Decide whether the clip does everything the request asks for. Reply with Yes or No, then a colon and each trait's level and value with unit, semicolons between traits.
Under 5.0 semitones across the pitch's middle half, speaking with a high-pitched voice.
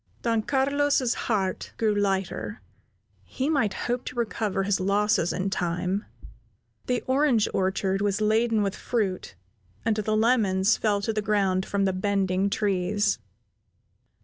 Yes: average, 3.0 semitones; high, 205 Hz